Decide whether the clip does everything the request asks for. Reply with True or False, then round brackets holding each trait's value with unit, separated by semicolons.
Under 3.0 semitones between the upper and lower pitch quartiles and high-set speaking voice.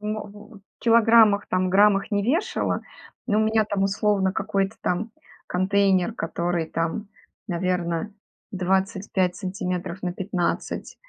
True (2.5 semitones; 195 Hz)